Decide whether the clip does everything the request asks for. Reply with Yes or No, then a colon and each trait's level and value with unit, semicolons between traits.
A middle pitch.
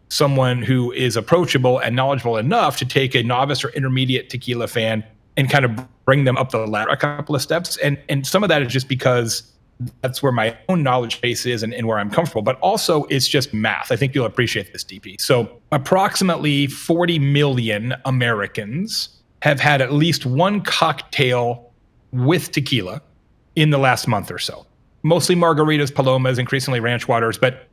No: low, 130 Hz